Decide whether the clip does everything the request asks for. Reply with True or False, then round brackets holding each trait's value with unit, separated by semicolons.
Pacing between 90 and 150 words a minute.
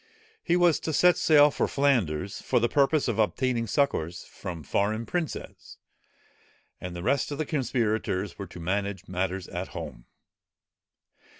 True (145 wpm)